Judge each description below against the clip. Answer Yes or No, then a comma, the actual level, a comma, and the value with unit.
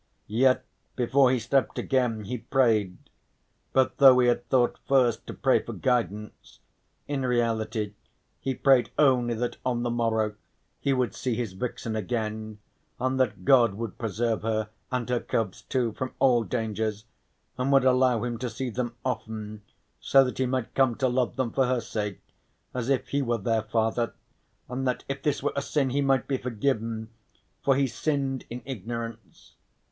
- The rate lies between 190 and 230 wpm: No, average, 175 wpm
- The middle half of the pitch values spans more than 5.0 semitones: No, average, 2.8 semitones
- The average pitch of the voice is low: Yes, low, 120 Hz